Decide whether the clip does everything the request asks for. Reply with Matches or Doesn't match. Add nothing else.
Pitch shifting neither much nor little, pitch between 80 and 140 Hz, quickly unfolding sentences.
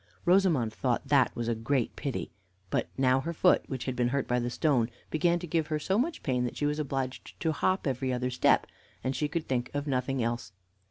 Matches